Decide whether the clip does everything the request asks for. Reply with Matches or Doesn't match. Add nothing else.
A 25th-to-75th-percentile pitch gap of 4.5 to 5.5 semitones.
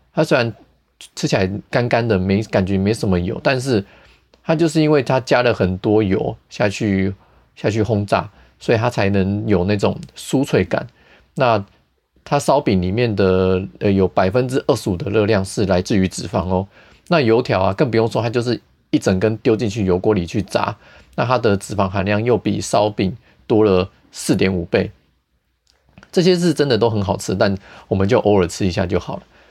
Doesn't match